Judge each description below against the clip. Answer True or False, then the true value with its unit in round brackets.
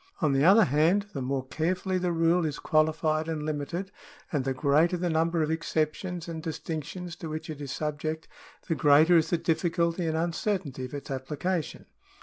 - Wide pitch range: False (2.5 semitones)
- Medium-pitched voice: True (160 Hz)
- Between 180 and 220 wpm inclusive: True (185 wpm)